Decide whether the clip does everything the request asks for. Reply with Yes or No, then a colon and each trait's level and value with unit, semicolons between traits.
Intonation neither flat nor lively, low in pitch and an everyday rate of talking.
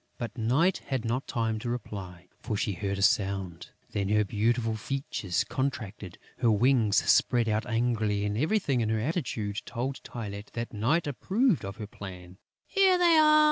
Yes: average, 4.4 semitones; low, 115 Hz; average, 170 wpm